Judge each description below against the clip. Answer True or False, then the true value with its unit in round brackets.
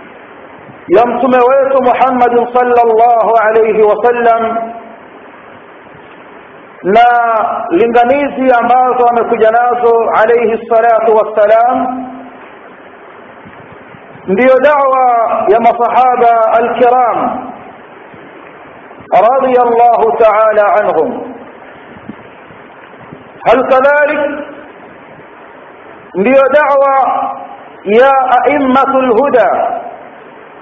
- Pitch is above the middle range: True (245 Hz)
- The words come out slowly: True (55 wpm)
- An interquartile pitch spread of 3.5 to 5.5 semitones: False (2.7 semitones)